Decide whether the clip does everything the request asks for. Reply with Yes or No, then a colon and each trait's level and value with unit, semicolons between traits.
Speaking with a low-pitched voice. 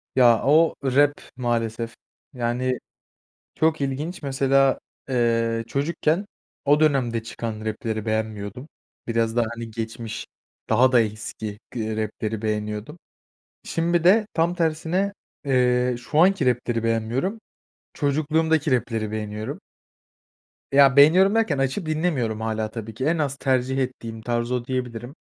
Yes: low, 125 Hz